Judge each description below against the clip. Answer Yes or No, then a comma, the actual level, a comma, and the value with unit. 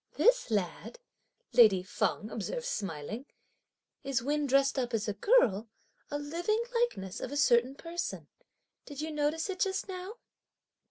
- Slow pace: No, average, 145 wpm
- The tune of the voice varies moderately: No, wide, 8.4 semitones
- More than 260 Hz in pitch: Yes, very high, 280 Hz